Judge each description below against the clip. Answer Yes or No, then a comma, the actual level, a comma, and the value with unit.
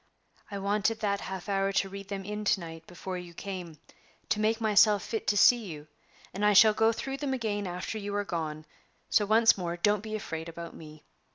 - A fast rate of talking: Yes, fast, 210 wpm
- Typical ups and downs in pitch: Yes, average, 3.3 semitones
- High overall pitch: Yes, high, 200 Hz